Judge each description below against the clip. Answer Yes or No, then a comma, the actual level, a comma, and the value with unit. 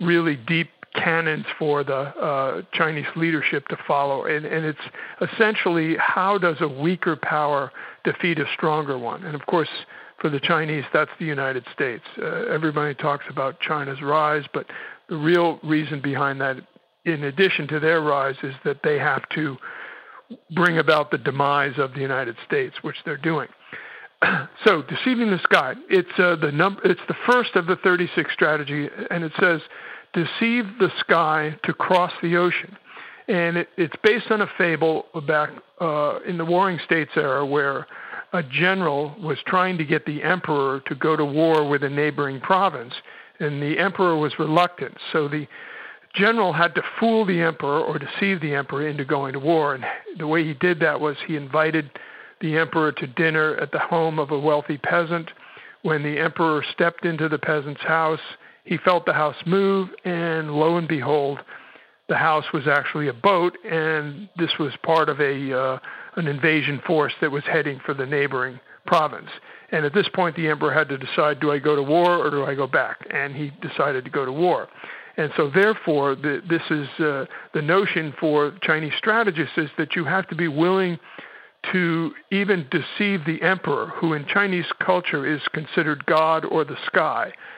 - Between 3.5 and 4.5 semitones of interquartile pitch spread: No, average, 3.1 semitones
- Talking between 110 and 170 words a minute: No, average, 180 wpm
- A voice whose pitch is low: No, medium, 160 Hz